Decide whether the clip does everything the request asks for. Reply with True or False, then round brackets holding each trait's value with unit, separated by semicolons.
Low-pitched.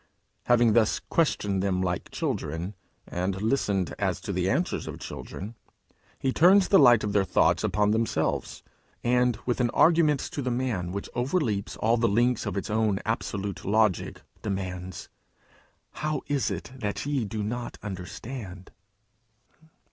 True (110 Hz)